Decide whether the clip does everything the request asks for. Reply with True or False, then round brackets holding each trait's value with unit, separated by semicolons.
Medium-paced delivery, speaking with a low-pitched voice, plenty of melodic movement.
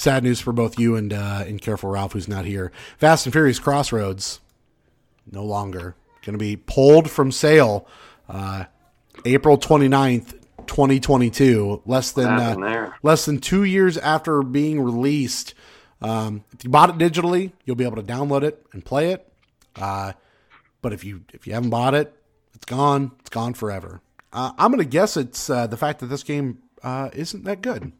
True (185 wpm; 125 Hz; 5.7 semitones)